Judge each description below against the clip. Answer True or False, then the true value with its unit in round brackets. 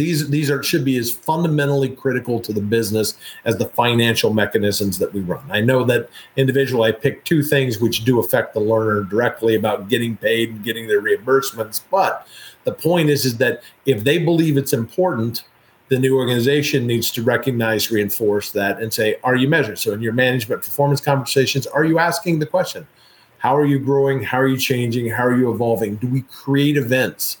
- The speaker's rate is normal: True (195 wpm)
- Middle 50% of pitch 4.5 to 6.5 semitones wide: False (3.5 semitones)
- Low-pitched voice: True (130 Hz)